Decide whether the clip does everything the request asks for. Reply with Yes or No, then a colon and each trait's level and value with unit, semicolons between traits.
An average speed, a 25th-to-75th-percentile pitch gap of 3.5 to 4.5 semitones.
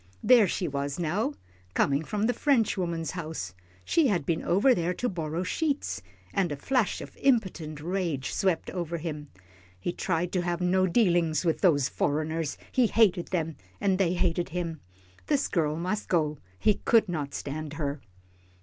Yes: average, 165 wpm; average, 3.9 semitones